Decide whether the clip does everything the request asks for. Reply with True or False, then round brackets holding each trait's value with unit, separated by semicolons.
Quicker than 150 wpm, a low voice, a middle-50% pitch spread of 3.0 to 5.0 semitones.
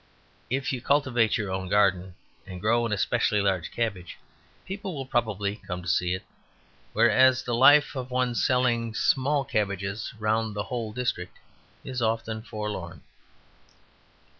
False (140 wpm; 110 Hz; 4.2 semitones)